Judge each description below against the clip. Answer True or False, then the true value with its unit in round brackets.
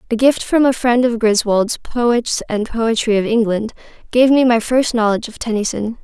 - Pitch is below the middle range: False (230 Hz)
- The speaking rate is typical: True (190 wpm)